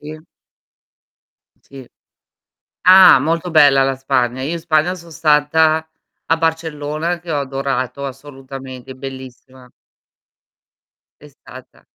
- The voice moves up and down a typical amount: Yes, average, 3.3 semitones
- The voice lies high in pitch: No, medium, 145 Hz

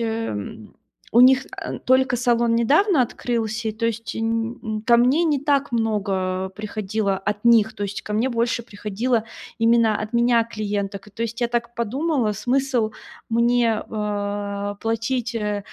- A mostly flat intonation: Yes, narrow, 2.3 semitones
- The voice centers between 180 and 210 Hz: No, high, 230 Hz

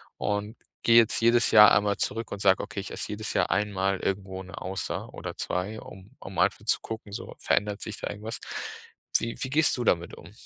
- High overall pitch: No, low, 105 Hz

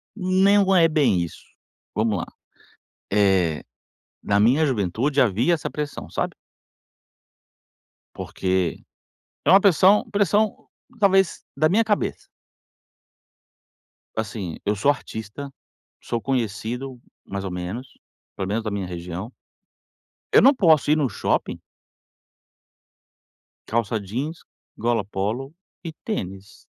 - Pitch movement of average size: No, wide, 8.0 semitones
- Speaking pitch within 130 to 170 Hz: No, low, 120 Hz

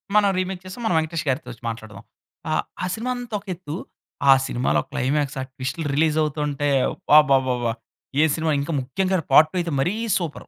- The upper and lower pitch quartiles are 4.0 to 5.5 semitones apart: Yes, average, 5.0 semitones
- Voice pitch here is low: No, medium, 150 Hz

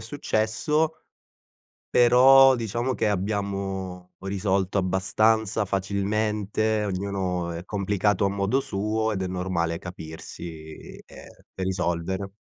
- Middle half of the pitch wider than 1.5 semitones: Yes, average, 2.8 semitones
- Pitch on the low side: Yes, low, 100 Hz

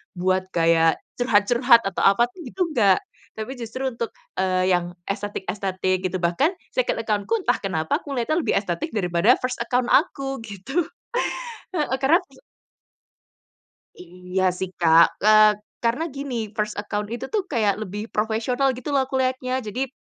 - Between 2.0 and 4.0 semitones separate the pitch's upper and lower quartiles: No, wide, 5.6 semitones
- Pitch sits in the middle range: No, high, 215 Hz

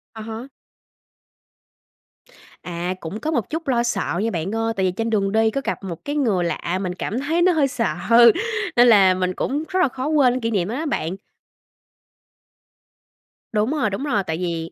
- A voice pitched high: Yes, high, 220 Hz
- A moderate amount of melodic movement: No, wide, 6.4 semitones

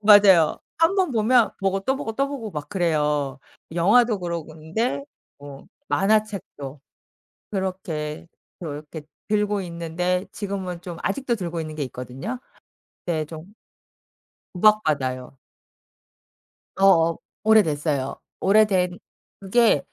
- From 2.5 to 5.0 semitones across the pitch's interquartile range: No, wide, 5.4 semitones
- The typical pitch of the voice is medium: Yes, medium, 180 Hz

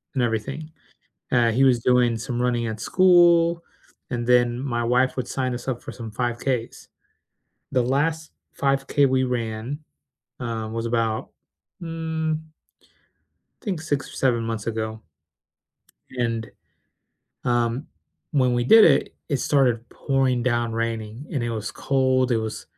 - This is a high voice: No, low, 125 Hz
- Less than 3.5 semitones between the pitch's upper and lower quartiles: Yes, average, 2.9 semitones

